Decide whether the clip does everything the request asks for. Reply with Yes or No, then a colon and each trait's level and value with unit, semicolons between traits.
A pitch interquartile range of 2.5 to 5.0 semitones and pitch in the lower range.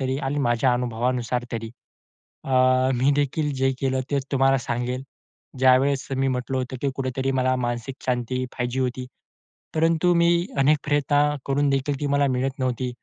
No: narrow, 1.8 semitones; low, 130 Hz